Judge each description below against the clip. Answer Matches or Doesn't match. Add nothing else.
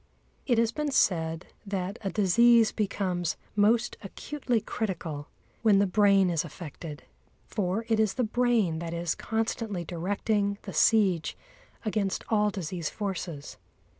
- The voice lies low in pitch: Doesn't match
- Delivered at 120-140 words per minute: Matches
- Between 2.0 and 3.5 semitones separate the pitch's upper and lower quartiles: Doesn't match